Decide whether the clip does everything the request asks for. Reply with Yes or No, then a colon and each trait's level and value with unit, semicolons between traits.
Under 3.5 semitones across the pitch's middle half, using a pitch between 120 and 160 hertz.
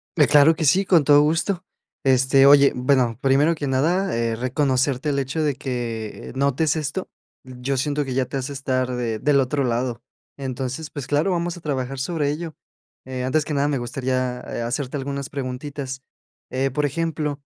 Yes: narrow, 2.5 semitones; medium, 140 Hz